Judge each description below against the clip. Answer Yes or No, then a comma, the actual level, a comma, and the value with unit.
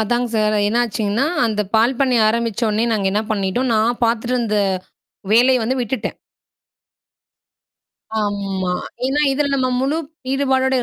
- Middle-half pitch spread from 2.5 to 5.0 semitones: Yes, average, 3.3 semitones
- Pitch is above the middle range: Yes, high, 230 Hz